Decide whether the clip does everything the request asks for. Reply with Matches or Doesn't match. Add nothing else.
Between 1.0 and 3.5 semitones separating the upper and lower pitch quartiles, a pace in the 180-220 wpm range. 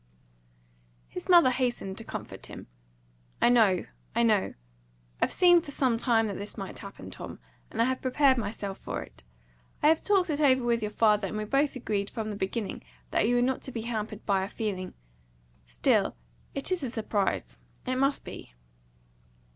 Doesn't match